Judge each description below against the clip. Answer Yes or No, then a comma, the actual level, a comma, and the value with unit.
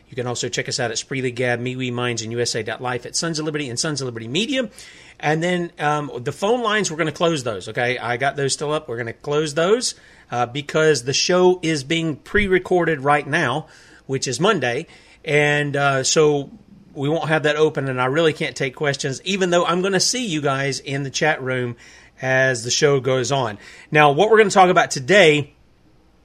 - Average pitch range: Yes, average, 4.2 semitones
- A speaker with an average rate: No, fast, 220 wpm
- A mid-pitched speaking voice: Yes, medium, 150 Hz